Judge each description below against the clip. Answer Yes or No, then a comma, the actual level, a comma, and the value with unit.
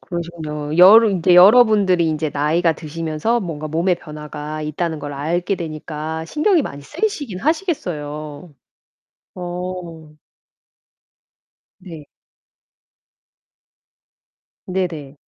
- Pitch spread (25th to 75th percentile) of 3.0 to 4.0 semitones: Yes, average, 3.3 semitones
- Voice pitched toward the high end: No, medium, 165 Hz